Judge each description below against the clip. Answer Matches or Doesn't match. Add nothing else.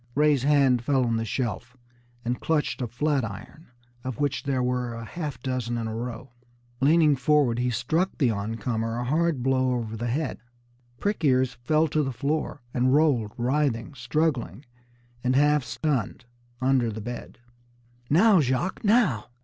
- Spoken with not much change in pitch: Doesn't match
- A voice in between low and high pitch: Doesn't match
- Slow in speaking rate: Doesn't match